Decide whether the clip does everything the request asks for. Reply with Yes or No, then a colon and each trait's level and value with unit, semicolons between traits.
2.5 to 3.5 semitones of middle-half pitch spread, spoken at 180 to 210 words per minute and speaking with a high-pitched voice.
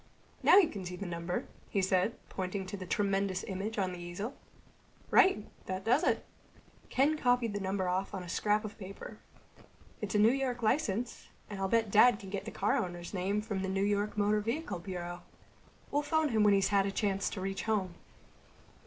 Yes: average, 2.8 semitones; average, 200 wpm; high, 200 Hz